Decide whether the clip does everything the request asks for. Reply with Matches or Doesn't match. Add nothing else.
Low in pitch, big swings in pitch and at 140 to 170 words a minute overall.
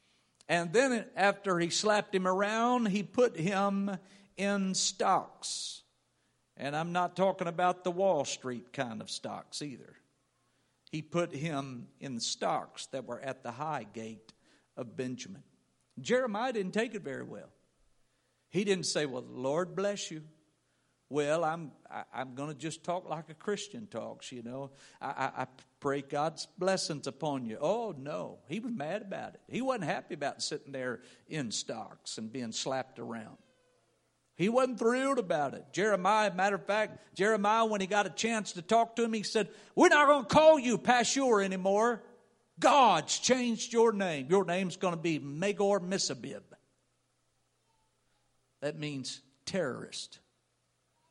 Doesn't match